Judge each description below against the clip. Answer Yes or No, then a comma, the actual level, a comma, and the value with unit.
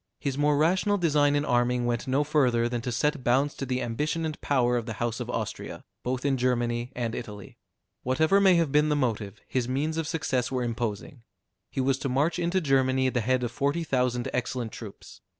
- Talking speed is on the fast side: Yes, fast, 210 wpm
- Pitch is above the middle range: No, low, 130 Hz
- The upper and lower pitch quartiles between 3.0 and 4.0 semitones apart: Yes, average, 3.6 semitones